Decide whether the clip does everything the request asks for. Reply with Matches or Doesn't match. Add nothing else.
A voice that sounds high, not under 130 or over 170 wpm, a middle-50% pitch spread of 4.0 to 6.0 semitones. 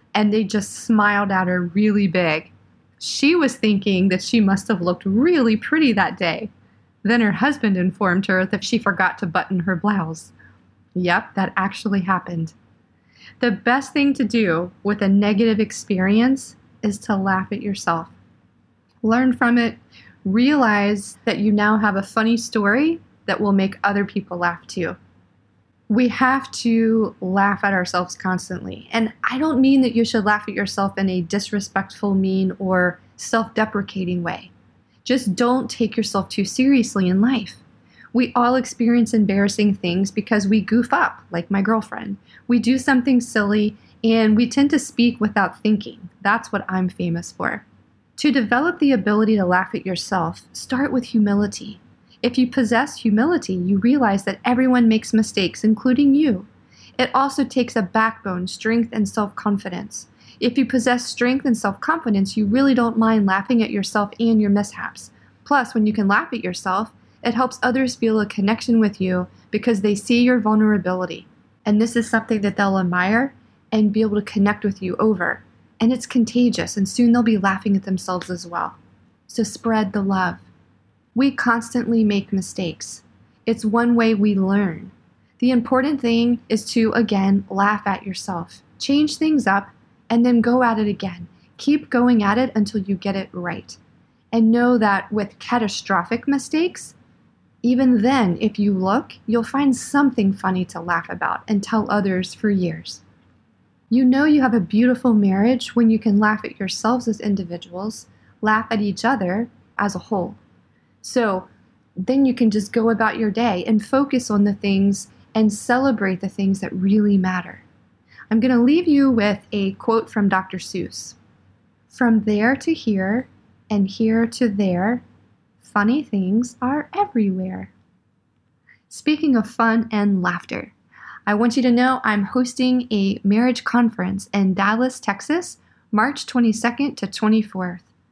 Doesn't match